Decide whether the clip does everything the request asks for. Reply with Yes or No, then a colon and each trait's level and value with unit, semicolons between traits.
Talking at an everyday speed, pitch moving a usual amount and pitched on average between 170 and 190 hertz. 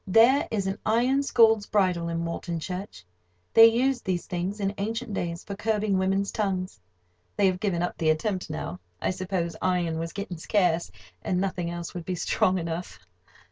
Yes: average, 180 wpm; average, 3.3 semitones; medium, 185 Hz